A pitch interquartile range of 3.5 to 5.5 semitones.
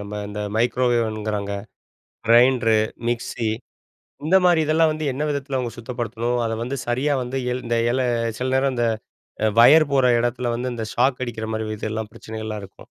No: average, 2.8 semitones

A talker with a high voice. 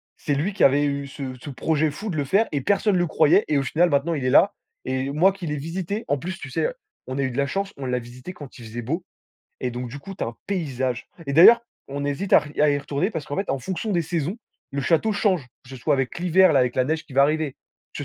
No: medium, 145 Hz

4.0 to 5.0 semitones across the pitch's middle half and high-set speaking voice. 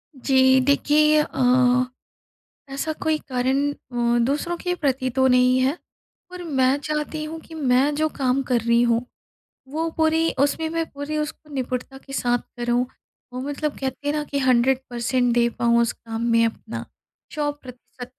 No: average, 3.3 semitones; very high, 265 Hz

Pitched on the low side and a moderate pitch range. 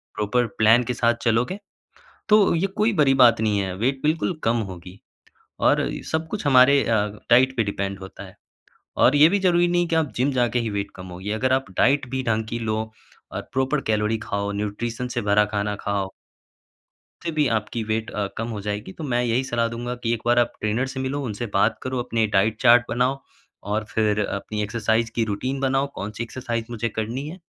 Yes: low, 115 Hz; average, 3.7 semitones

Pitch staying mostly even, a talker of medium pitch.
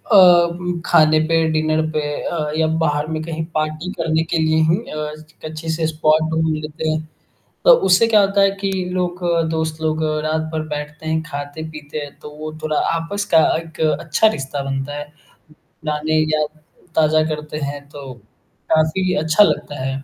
Yes: narrow, 1.3 semitones; medium, 155 Hz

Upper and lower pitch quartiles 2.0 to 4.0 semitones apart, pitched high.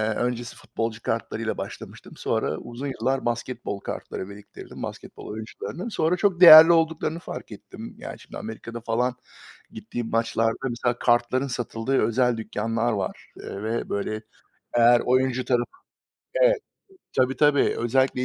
No: average, 2.7 semitones; low, 120 Hz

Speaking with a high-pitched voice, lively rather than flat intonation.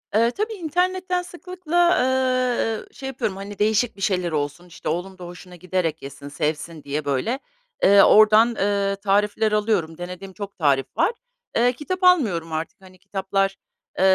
Yes: high, 200 Hz; wide, 6.3 semitones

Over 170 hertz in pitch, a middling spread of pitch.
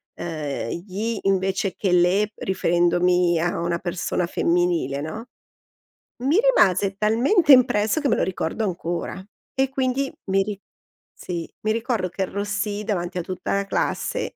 Yes: high, 190 Hz; average, 3.6 semitones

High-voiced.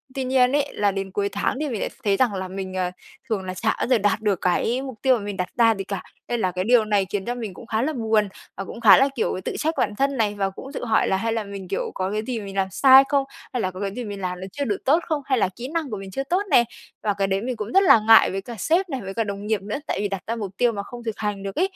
Yes: high, 215 Hz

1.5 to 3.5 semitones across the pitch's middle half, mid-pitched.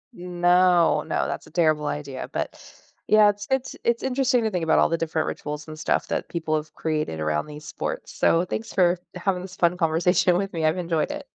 Yes: average, 3.0 semitones; medium, 175 Hz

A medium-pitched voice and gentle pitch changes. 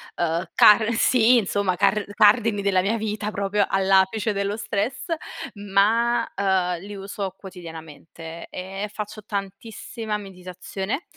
No: high, 200 Hz; narrow, 2.0 semitones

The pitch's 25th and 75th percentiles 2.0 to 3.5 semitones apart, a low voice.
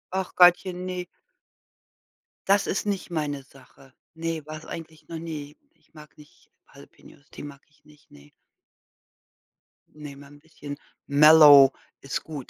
No: narrow, 2.5 semitones; medium, 150 Hz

